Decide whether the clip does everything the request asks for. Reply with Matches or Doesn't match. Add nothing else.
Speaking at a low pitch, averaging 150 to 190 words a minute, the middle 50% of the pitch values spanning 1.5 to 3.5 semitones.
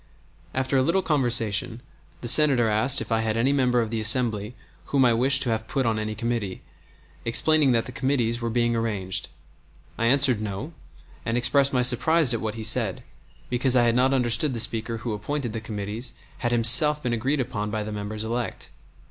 Doesn't match